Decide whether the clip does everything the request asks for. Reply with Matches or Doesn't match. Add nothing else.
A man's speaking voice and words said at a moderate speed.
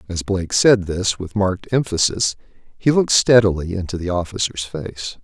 Matches